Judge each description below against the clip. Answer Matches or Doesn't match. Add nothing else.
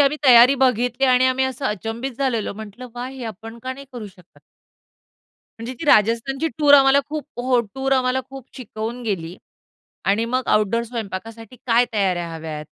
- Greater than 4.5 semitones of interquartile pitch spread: Doesn't match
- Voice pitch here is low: Doesn't match